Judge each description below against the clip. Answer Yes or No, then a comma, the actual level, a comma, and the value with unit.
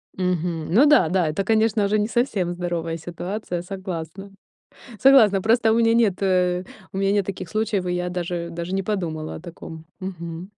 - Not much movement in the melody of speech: No, average, 3.3 semitones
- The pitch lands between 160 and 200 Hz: Yes, medium, 185 Hz